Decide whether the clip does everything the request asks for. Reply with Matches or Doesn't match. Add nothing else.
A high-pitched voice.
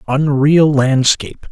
Doesn't match